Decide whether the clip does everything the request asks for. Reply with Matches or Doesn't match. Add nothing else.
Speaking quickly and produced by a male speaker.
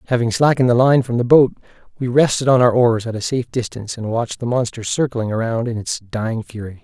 Matches